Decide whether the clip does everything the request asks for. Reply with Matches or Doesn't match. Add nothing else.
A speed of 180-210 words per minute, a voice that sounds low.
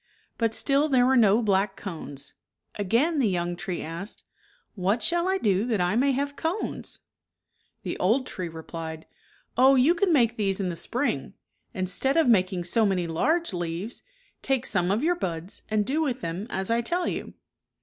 Doesn't match